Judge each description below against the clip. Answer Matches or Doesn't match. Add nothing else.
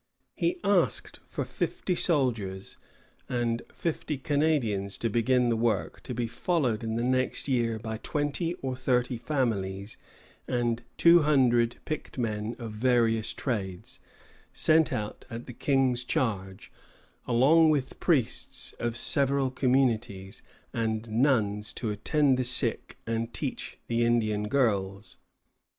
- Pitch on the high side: Doesn't match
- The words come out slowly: Matches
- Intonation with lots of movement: Doesn't match